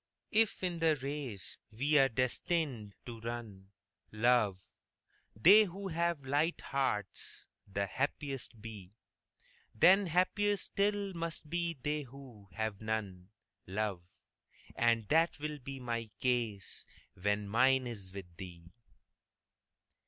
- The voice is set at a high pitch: No, low, 125 Hz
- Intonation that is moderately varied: No, wide, 7.1 semitones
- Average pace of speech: No, slow, 115 wpm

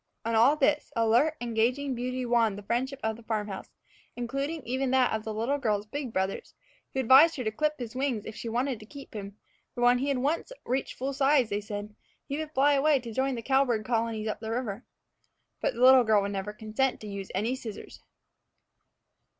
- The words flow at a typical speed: No, fast, 215 wpm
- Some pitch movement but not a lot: Yes, average, 3.7 semitones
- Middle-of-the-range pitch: No, high, 240 Hz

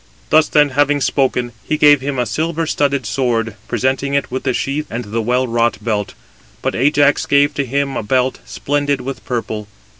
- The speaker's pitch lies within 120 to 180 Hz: Yes, low, 135 Hz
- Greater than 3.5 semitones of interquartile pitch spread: No, average, 3.1 semitones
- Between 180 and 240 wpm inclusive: Yes, average, 185 wpm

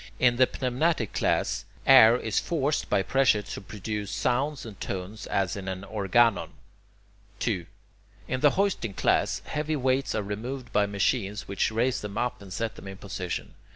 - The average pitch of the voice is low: Yes, low, 110 Hz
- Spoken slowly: No, average, 170 wpm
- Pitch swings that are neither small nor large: Yes, average, 4.4 semitones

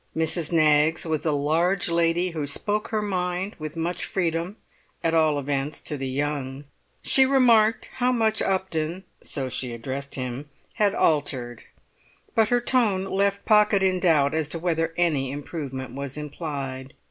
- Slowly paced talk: No, average, 155 wpm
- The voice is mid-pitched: Yes, medium, 160 Hz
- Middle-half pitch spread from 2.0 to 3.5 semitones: No, average, 5.0 semitones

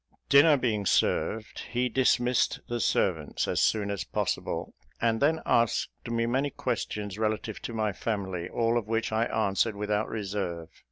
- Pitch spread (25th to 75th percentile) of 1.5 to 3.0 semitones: Yes, narrow, 2.6 semitones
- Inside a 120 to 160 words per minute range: Yes, average, 155 wpm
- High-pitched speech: No, low, 110 Hz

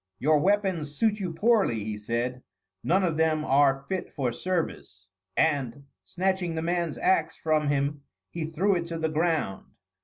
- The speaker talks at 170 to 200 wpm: No, average, 160 wpm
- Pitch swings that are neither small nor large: Yes, average, 4.2 semitones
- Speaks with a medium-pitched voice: Yes, medium, 160 Hz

